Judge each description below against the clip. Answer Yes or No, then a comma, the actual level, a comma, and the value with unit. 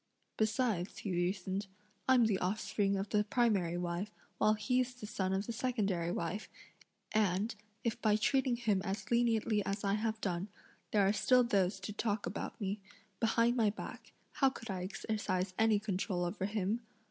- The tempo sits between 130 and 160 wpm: No, average, 170 wpm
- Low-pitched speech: No, high, 210 Hz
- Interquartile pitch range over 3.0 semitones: No, average, 2.7 semitones